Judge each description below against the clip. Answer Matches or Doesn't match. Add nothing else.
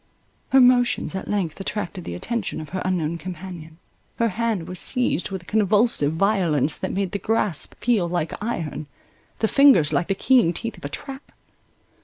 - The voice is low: Doesn't match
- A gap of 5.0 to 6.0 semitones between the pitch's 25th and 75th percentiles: Matches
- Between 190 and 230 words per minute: Doesn't match